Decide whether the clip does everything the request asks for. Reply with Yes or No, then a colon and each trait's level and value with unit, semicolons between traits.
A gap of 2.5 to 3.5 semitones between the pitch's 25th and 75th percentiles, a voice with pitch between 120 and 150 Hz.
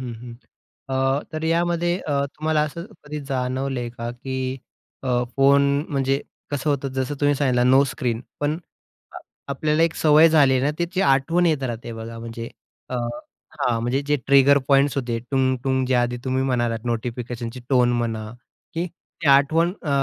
Yes: average, 3.2 semitones; low, 135 Hz